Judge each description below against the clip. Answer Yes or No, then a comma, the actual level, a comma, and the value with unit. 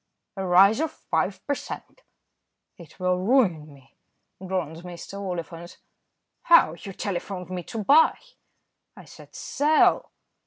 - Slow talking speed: Yes, slow, 120 wpm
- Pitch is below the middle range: No, medium, 185 Hz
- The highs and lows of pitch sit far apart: No, average, 3.8 semitones